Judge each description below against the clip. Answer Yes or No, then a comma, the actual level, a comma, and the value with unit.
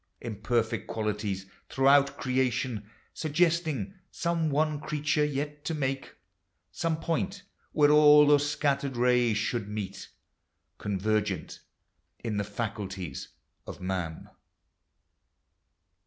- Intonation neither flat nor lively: No, wide, 5.9 semitones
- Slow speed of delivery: Yes, slow, 95 wpm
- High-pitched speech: No, low, 130 Hz